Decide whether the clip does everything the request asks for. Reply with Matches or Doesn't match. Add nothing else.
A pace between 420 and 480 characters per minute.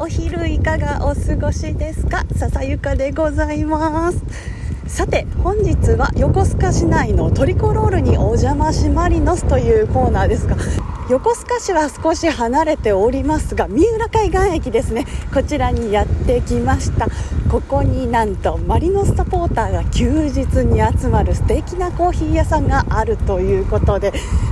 Doesn't match